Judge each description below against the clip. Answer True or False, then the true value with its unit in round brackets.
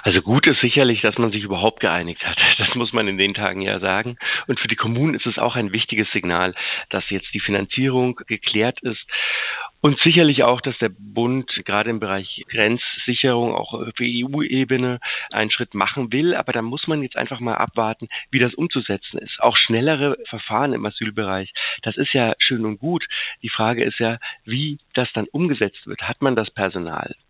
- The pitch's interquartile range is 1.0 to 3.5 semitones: False (3.9 semitones)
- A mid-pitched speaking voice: False (115 Hz)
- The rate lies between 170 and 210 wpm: True (190 wpm)